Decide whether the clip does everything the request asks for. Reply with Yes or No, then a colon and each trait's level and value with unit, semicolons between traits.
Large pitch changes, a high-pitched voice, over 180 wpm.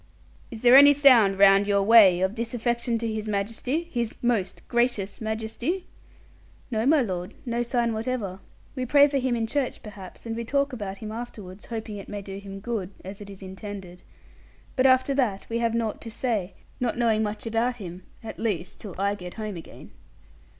No: average, 3.4 semitones; high, 225 Hz; average, 190 wpm